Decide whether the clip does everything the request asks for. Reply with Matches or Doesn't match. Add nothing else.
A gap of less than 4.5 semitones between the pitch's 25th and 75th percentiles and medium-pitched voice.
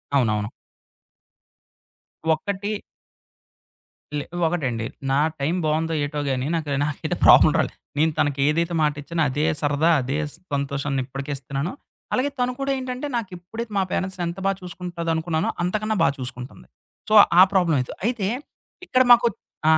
Doesn't match